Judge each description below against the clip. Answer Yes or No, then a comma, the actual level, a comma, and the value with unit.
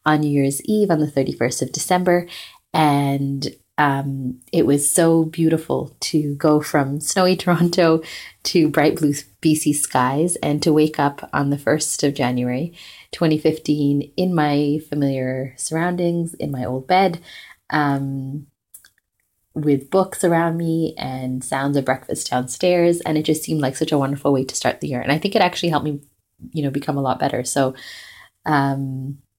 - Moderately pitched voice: Yes, medium, 145 Hz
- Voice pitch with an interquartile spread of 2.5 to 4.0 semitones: Yes, average, 2.9 semitones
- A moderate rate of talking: Yes, average, 165 wpm